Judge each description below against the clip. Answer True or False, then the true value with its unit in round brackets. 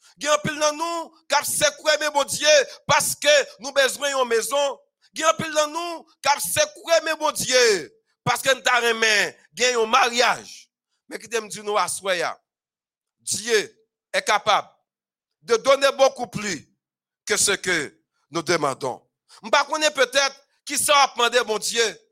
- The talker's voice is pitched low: False (275 Hz)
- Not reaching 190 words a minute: True (170 wpm)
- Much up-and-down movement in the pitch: False (4.7 semitones)